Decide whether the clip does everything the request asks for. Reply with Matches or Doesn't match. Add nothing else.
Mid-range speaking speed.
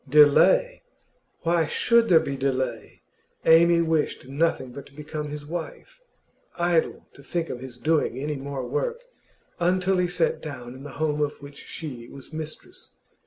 Matches